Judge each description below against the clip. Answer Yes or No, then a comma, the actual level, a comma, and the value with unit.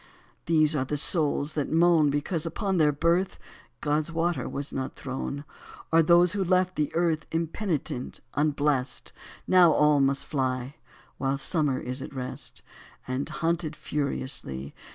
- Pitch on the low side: No, medium, 150 Hz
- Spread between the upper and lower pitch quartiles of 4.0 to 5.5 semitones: No, average, 3.3 semitones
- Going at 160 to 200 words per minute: No, average, 140 wpm